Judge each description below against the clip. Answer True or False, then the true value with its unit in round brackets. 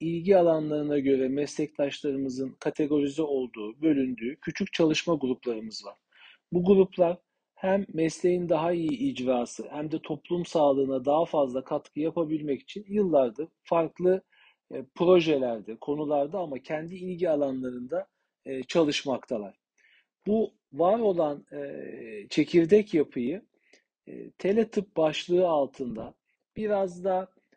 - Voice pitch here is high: False (155 Hz)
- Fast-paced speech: False (100 wpm)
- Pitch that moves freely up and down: False (4.6 semitones)